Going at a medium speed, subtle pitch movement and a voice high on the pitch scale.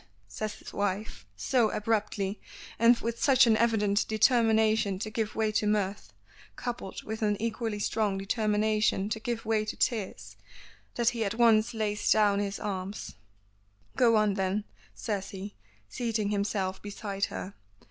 Yes: average, 145 wpm; narrow, 1.9 semitones; high, 215 Hz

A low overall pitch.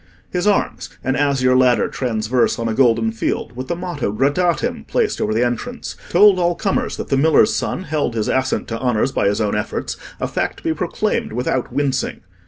Yes: low, 130 Hz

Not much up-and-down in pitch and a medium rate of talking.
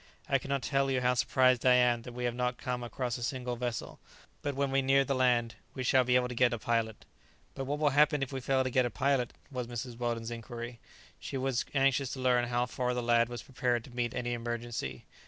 No: narrow, 1.7 semitones; fast, 240 wpm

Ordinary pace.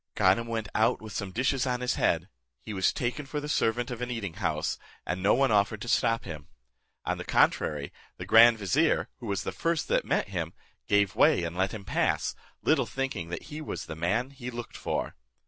No: fast, 215 wpm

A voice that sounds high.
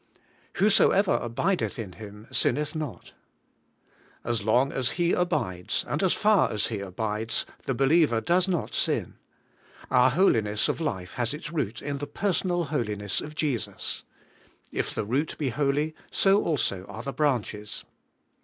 No: low, 135 Hz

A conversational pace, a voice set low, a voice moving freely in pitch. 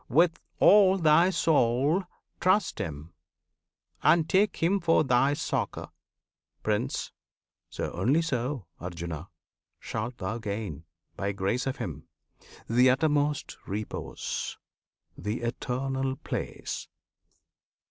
No: slow, 100 wpm; low, 130 Hz; wide, 7.6 semitones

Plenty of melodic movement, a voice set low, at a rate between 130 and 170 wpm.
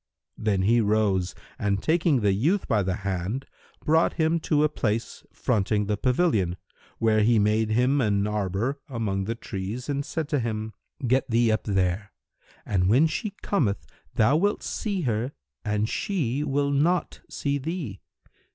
Yes: wide, 5.7 semitones; low, 115 Hz; average, 160 wpm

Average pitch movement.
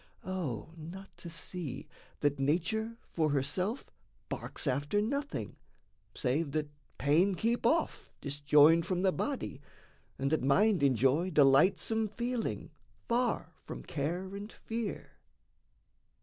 No: wide, 6.5 semitones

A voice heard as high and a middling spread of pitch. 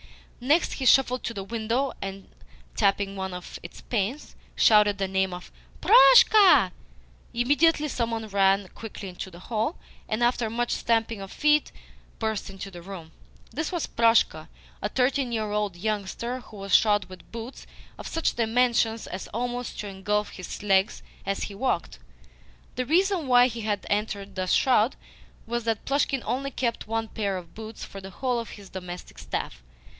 Yes: high, 220 Hz; average, 4.0 semitones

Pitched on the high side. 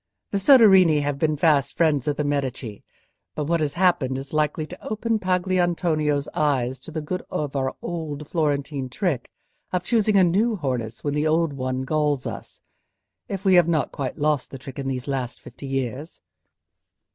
No: medium, 150 Hz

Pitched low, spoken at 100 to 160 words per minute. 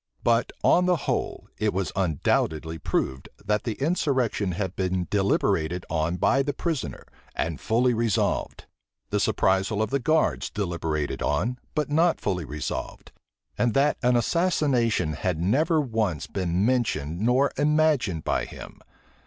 Yes: low, 110 Hz; average, 140 wpm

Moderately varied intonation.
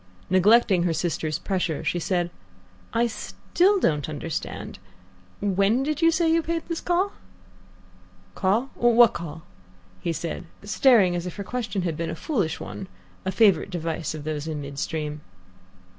No: wide, 6.7 semitones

